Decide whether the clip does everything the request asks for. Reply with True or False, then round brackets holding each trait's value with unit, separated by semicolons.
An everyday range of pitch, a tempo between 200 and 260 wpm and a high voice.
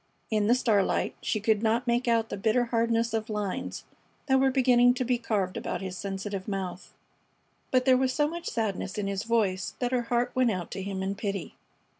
True (3.8 semitones; 205 wpm; 225 Hz)